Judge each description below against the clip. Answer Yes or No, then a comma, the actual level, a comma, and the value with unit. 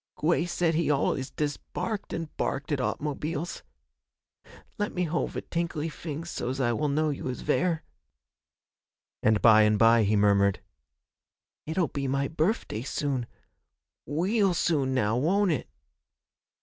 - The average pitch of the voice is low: No, medium, 150 Hz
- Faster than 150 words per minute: No, average, 140 wpm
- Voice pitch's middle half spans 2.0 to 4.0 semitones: No, average, 4.7 semitones